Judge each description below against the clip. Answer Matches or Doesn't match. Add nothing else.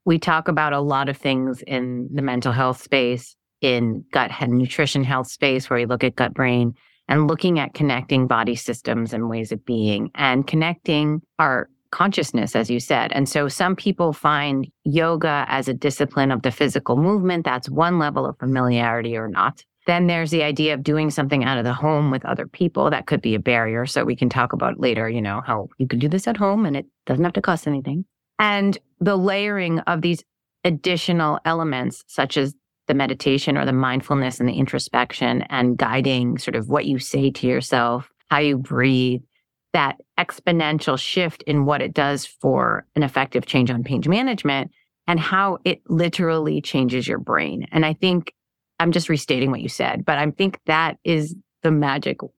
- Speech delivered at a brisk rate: Doesn't match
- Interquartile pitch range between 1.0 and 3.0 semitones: Doesn't match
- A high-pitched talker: Doesn't match